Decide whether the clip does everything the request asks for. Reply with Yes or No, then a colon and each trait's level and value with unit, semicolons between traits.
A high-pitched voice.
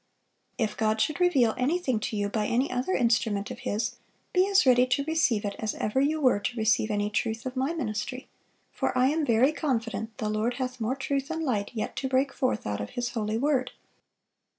Yes: high, 245 Hz